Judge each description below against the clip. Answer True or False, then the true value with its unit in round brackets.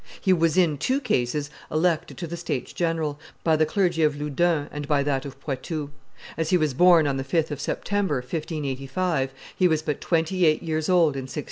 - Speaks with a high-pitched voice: False (155 Hz)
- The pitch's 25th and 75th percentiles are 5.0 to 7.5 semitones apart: False (3.1 semitones)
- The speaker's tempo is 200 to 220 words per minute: True (205 wpm)